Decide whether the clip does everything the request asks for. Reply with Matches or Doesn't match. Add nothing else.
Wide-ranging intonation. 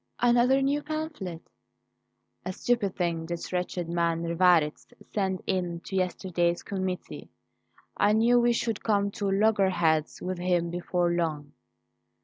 Doesn't match